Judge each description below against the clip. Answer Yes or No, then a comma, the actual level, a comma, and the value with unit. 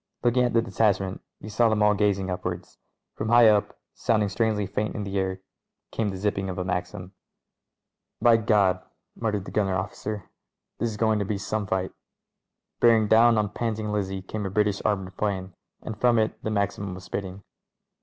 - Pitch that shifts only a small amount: Yes, narrow, 2.2 semitones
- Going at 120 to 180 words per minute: No, average, 195 wpm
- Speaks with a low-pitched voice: Yes, low, 105 Hz